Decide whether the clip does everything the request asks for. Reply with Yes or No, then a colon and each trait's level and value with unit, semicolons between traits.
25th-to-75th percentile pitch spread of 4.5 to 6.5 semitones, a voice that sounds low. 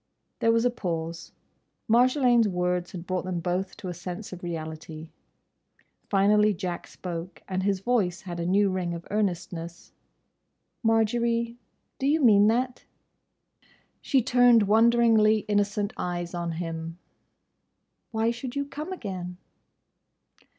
No: average, 4.8 semitones; high, 200 Hz